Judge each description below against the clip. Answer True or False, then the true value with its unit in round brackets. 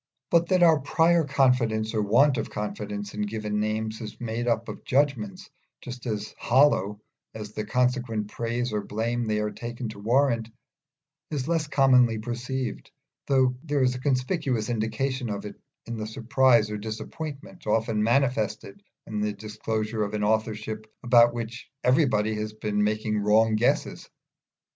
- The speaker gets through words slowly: False (155 wpm)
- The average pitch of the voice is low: True (115 Hz)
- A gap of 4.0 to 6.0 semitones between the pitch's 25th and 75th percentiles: False (3.2 semitones)